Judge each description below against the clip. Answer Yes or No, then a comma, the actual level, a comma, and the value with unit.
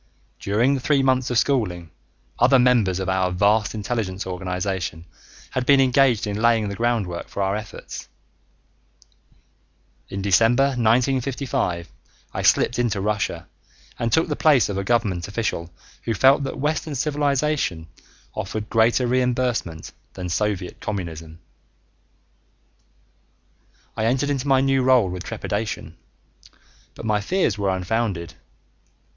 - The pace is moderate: No, slow, 130 wpm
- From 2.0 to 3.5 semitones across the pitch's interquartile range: No, average, 5.2 semitones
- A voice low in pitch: Yes, low, 110 Hz